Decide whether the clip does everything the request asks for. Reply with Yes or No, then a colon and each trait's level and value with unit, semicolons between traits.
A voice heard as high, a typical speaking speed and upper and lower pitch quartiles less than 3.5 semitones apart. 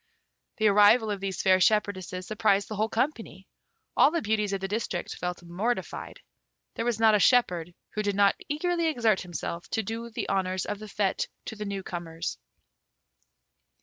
Yes: high, 205 Hz; average, 175 wpm; average, 2.9 semitones